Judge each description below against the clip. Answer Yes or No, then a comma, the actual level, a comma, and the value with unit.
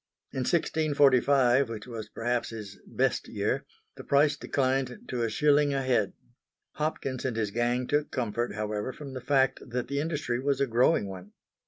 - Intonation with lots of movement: No, average, 3.4 semitones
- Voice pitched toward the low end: Yes, low, 130 Hz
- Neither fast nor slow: Yes, average, 170 wpm